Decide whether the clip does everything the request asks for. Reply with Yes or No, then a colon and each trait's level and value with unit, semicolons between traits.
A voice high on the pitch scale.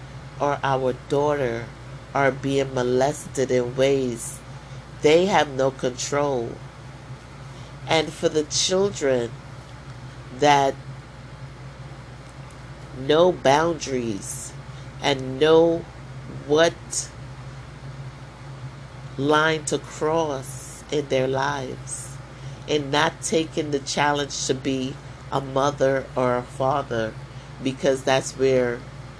No: low, 135 Hz